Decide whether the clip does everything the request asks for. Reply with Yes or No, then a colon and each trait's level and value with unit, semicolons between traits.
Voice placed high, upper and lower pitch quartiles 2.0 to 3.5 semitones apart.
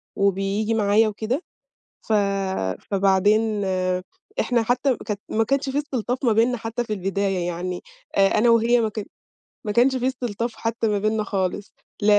Yes: high, 220 Hz; average, 3.1 semitones